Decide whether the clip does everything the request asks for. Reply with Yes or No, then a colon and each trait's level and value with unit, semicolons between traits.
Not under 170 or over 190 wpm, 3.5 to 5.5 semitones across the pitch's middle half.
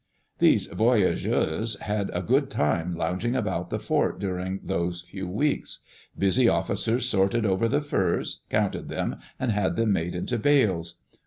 No: average, 150 wpm; average, 4.7 semitones